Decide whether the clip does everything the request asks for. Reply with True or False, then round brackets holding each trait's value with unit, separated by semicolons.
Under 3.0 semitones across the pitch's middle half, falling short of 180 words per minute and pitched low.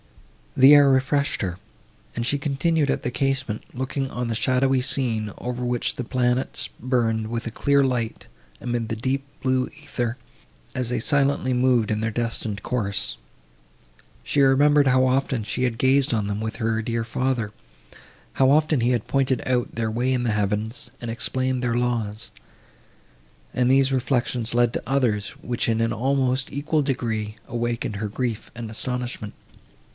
True (2.6 semitones; 165 wpm; 125 Hz)